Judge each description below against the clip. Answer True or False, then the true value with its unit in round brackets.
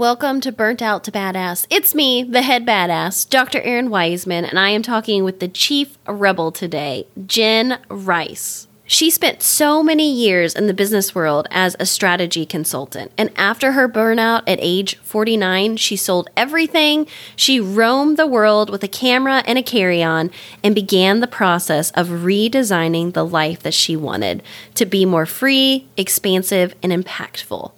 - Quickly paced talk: False (165 wpm)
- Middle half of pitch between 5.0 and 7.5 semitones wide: True (5.6 semitones)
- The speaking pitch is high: True (205 Hz)